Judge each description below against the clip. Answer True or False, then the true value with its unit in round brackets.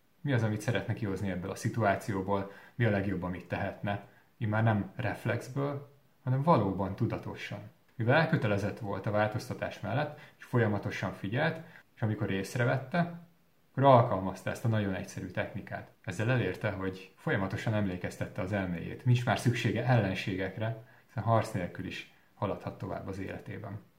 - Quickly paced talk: False (145 wpm)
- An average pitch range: True (4.1 semitones)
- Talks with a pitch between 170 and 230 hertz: False (110 Hz)